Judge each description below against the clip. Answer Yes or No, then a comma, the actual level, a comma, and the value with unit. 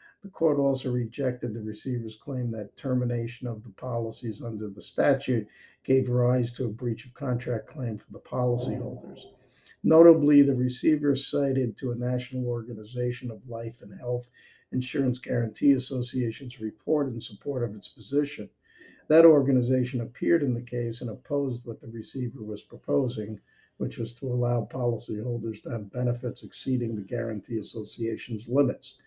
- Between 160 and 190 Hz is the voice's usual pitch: No, low, 125 Hz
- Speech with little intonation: Yes, narrow, 2.3 semitones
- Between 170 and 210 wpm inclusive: No, average, 150 wpm